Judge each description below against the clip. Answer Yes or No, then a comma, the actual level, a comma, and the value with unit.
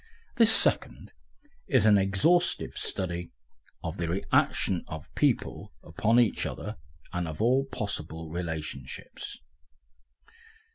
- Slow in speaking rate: Yes, slow, 105 wpm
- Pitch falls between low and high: No, very low, 95 Hz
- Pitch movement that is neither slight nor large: No, wide, 5.8 semitones